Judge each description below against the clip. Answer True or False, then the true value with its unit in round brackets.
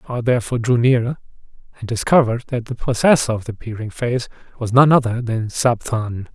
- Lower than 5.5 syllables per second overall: False (5.6 syllables/s)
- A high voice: False (120 Hz)